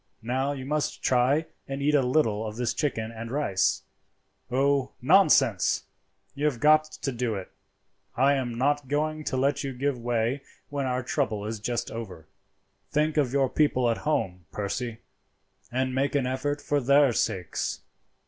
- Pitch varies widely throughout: No, average, 3.6 semitones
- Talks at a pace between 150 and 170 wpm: Yes, average, 165 wpm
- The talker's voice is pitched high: No, low, 130 Hz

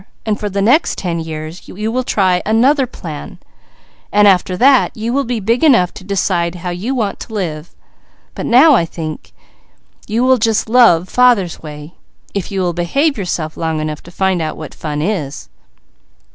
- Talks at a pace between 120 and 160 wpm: No, average, 175 wpm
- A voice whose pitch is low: No, high, 190 Hz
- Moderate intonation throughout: No, wide, 5.7 semitones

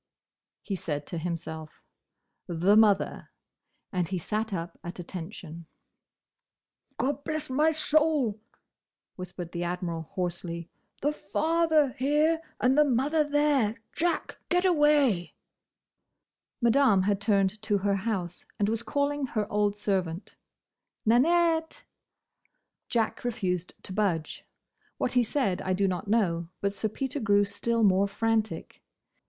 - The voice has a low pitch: No, high, 210 Hz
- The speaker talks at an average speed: No, slow, 120 wpm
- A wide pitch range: Yes, wide, 7.3 semitones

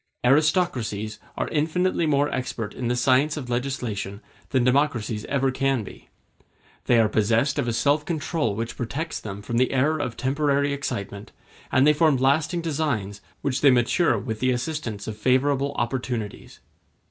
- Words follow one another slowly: No, average, 160 wpm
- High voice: No, low, 130 Hz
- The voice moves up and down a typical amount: Yes, average, 4.0 semitones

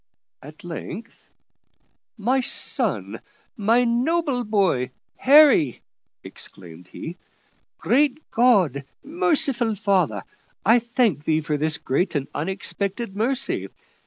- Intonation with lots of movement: Yes, wide, 7.8 semitones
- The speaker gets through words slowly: Yes, slow, 100 wpm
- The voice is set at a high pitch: Yes, high, 210 Hz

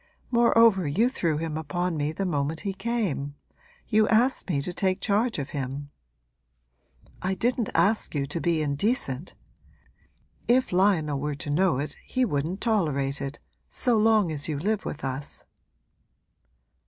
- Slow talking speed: No, average, 150 wpm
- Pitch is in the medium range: Yes, medium, 175 Hz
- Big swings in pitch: Yes, wide, 6.8 semitones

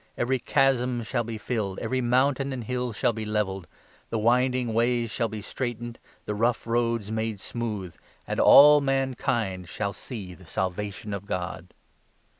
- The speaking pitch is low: Yes, low, 115 Hz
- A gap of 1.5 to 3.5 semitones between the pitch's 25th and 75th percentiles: Yes, average, 3.1 semitones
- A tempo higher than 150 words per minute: Yes, average, 160 wpm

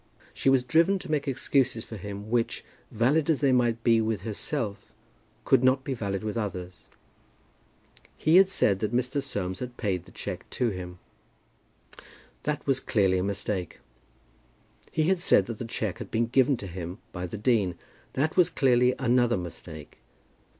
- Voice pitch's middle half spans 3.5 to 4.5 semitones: No, average, 5.1 semitones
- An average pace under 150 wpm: No, average, 170 wpm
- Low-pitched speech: Yes, low, 115 Hz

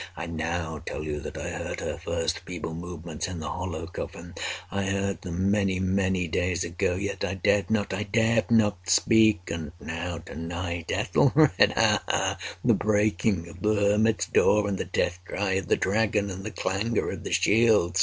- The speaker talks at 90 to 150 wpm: No, average, 165 wpm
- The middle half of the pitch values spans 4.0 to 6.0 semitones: No, average, 3.2 semitones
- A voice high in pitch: No, very low, 95 Hz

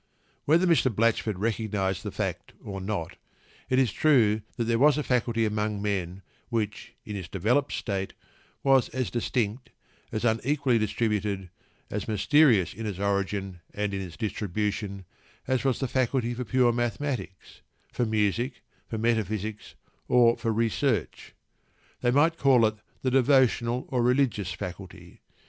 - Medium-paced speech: Yes, average, 145 wpm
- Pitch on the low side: Yes, low, 110 Hz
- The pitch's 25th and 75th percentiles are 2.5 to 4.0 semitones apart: Yes, average, 3.7 semitones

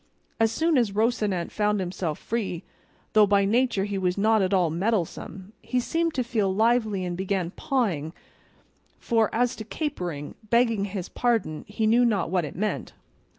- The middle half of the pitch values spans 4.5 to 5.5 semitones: No, average, 3.9 semitones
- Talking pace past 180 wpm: No, average, 165 wpm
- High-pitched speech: Yes, high, 210 Hz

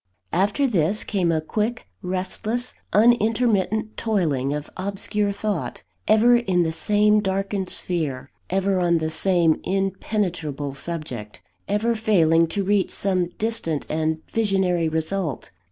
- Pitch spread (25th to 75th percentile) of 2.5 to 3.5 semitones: No, average, 4.5 semitones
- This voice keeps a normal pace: No, slow, 120 wpm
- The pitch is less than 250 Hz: Yes, high, 190 Hz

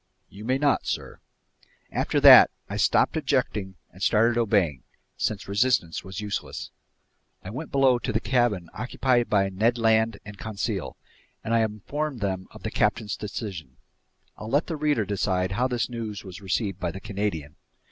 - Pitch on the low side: Yes, low, 105 Hz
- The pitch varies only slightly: No, average, 3.7 semitones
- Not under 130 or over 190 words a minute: Yes, average, 165 wpm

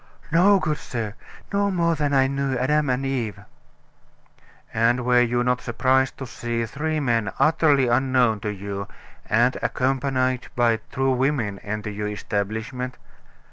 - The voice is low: Yes, low, 125 Hz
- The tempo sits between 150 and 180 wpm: No, average, 140 wpm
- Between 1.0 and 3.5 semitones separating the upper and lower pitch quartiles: Yes, average, 3.2 semitones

